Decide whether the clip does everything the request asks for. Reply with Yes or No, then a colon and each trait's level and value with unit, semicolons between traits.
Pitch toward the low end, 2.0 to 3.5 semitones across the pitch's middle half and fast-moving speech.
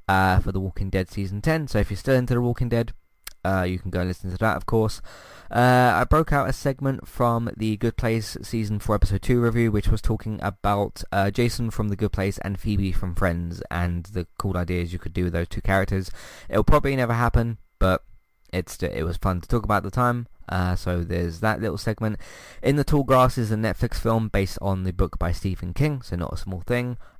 No: low, 105 Hz; average, 4.2 semitones; fast, 235 wpm